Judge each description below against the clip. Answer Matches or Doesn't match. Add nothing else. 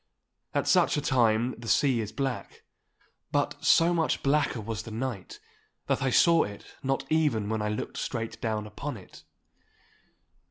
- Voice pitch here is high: Doesn't match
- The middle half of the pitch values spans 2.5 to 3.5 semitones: Doesn't match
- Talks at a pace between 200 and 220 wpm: Doesn't match